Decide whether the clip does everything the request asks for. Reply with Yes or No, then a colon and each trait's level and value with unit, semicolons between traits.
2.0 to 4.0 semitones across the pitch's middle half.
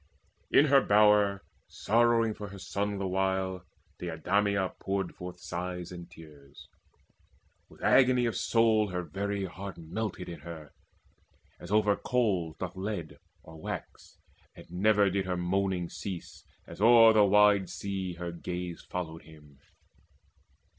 Yes: average, 2.8 semitones